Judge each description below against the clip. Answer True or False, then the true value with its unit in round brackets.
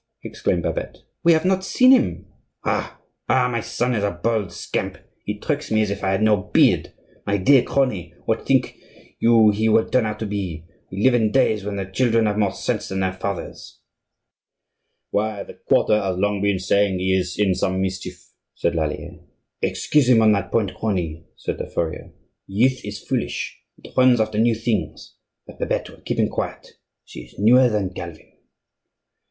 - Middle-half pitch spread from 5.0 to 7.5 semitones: False (3.6 semitones)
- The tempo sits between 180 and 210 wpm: True (185 wpm)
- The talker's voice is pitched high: False (105 Hz)